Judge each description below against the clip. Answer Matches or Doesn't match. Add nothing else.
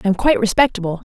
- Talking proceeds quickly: Matches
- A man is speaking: Doesn't match